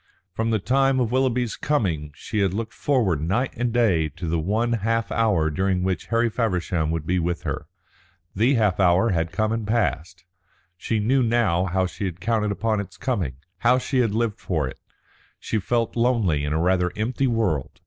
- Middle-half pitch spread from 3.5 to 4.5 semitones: No, average, 5.0 semitones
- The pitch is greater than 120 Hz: No, low, 105 Hz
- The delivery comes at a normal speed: Yes, average, 190 wpm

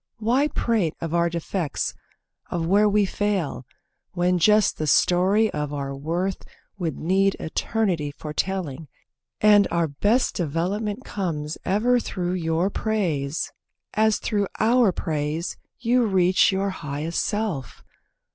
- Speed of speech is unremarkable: No, slow, 130 wpm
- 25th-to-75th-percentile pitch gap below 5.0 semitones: Yes, average, 4.5 semitones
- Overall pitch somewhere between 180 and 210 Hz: Yes, medium, 185 Hz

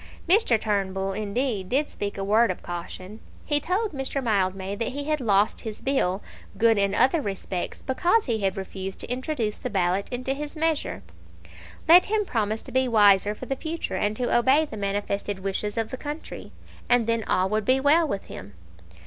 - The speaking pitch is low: No, high, 225 Hz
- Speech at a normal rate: Yes, average, 190 wpm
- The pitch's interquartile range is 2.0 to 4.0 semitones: No, wide, 5.5 semitones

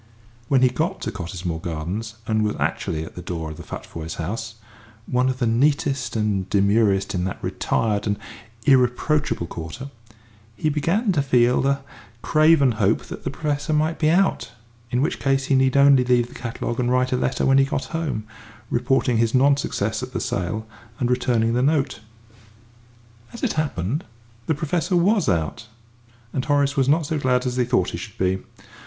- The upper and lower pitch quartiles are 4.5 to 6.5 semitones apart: Yes, average, 4.8 semitones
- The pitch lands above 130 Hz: No, low, 125 Hz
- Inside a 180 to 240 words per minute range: Yes, average, 185 wpm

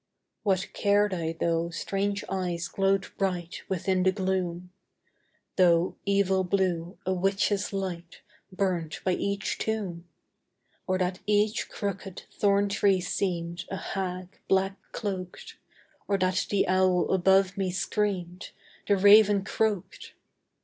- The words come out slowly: Yes, slow, 120 wpm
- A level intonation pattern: Yes, narrow, 1.8 semitones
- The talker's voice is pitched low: No, high, 190 Hz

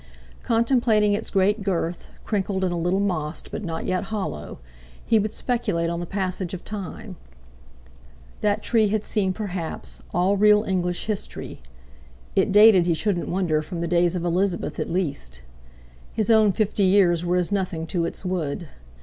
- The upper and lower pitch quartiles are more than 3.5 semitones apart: No, average, 3.2 semitones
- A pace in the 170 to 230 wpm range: No, average, 160 wpm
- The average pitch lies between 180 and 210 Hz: Yes, medium, 185 Hz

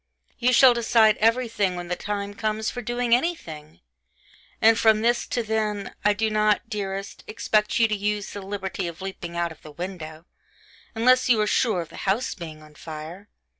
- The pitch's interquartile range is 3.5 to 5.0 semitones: Yes, average, 3.9 semitones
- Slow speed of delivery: No, average, 185 wpm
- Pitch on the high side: Yes, high, 210 Hz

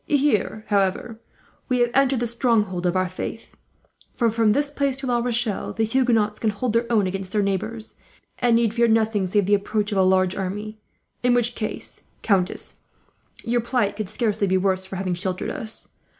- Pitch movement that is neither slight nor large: Yes, average, 3.4 semitones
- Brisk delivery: No, average, 190 wpm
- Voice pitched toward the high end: Yes, high, 215 Hz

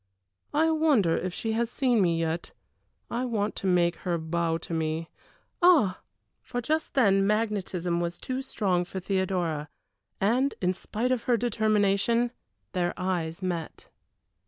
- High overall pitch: Yes, high, 195 Hz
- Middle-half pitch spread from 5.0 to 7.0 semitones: Yes, wide, 5.4 semitones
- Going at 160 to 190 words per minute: No, average, 145 wpm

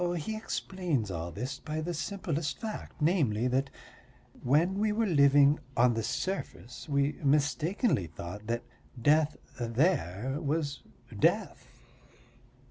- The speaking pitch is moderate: Yes, medium, 145 Hz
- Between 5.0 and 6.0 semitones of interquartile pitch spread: Yes, wide, 5.6 semitones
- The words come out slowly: Yes, slow, 120 wpm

